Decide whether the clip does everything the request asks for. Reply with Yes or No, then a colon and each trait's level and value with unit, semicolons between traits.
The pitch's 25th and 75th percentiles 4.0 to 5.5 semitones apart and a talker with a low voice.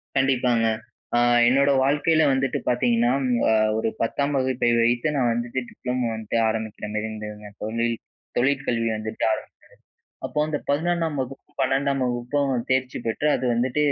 No: average, 3.0 semitones; low, 125 Hz